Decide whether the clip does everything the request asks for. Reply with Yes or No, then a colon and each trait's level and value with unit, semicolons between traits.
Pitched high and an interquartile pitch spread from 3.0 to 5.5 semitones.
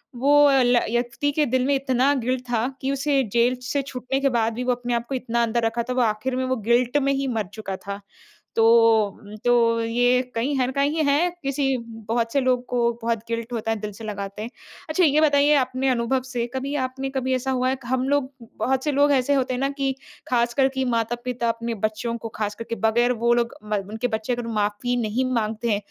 No: high, 245 Hz; narrow, 2.6 semitones